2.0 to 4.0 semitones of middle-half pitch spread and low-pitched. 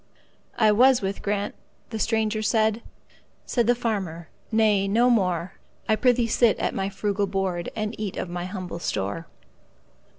No: average, 2.9 semitones; high, 210 Hz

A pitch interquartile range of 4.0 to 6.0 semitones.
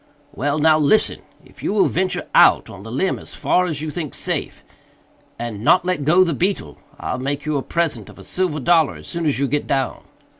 Yes: average, 4.3 semitones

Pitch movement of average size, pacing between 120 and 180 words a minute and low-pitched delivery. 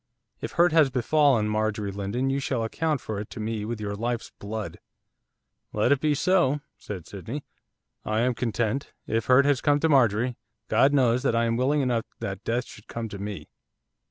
No: average, 4.3 semitones; average, 190 wpm; low, 120 Hz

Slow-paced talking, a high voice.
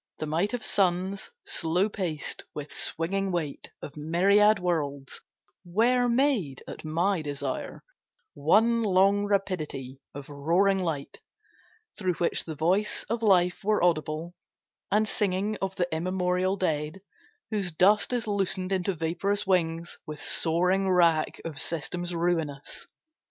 No: slow, 130 wpm; medium, 180 Hz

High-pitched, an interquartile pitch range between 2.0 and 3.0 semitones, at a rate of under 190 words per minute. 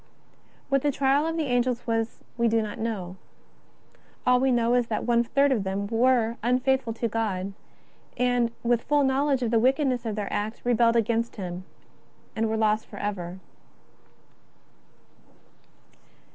Yes: high, 235 Hz; narrow, 2.6 semitones; average, 150 wpm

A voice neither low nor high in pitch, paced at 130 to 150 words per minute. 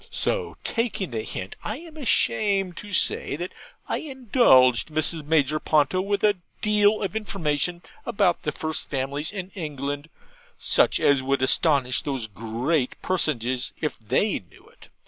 Yes: medium, 155 Hz; average, 145 wpm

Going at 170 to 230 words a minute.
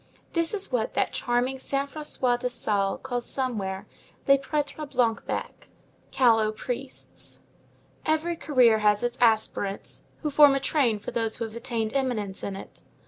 No: average, 155 wpm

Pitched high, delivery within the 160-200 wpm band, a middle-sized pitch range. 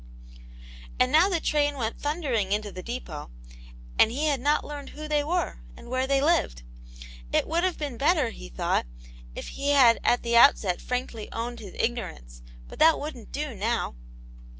Yes: very high, 255 Hz; average, 175 wpm; average, 4.8 semitones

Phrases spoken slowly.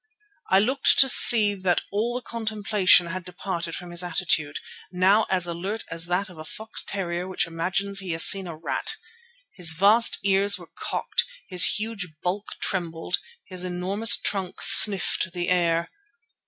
No: average, 160 wpm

